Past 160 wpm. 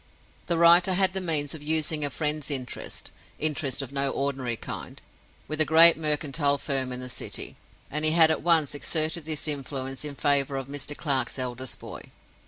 Yes: average, 175 wpm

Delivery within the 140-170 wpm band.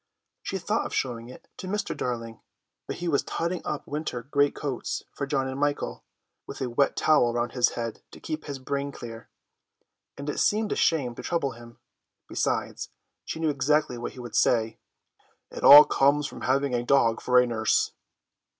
No: average, 185 wpm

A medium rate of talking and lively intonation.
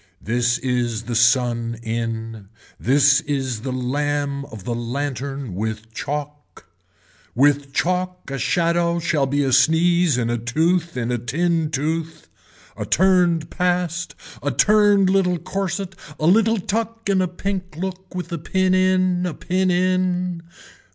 Yes: average, 145 wpm; wide, 6.2 semitones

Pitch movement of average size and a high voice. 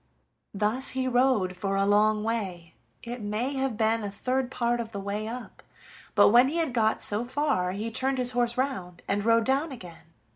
Yes: average, 4.0 semitones; high, 230 Hz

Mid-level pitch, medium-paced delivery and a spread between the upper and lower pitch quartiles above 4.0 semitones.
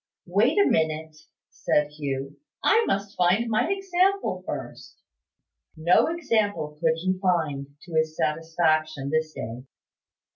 No: medium, 165 Hz; slow, 120 wpm; average, 4.9 semitones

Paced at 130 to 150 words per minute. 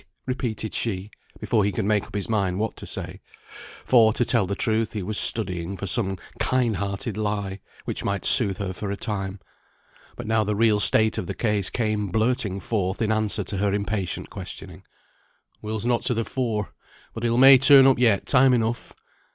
No: average, 195 wpm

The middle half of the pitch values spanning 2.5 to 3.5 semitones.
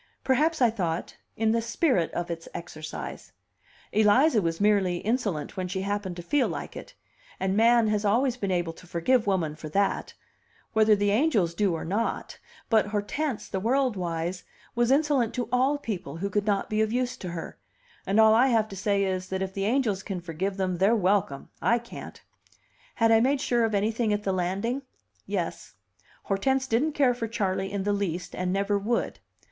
No: average, 4.1 semitones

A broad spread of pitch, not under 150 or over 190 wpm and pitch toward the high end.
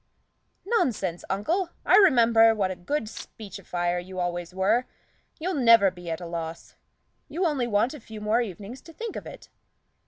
Yes: wide, 6.3 semitones; average, 165 wpm; high, 215 Hz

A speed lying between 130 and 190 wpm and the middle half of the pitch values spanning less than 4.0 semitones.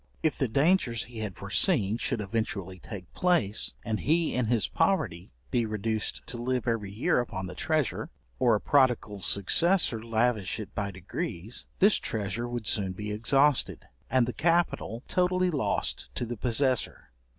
No: average, 160 wpm; average, 4.5 semitones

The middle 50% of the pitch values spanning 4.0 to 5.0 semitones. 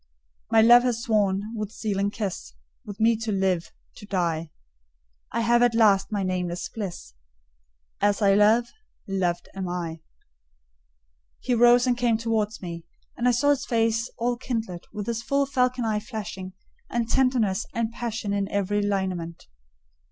No: average, 3.4 semitones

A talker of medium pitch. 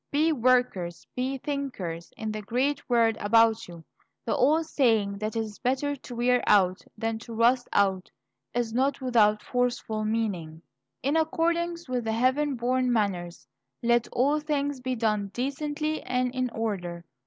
No: high, 240 Hz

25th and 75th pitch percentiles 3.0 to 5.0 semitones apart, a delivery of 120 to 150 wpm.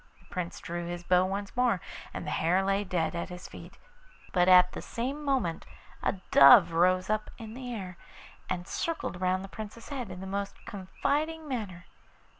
No: average, 4.4 semitones; average, 185 wpm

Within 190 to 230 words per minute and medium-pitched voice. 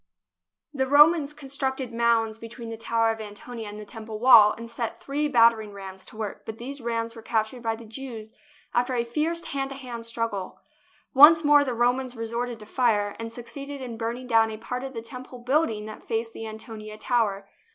No: average, 200 wpm; high, 230 Hz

